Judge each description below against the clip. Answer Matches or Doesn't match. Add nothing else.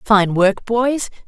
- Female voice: Matches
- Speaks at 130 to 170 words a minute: Matches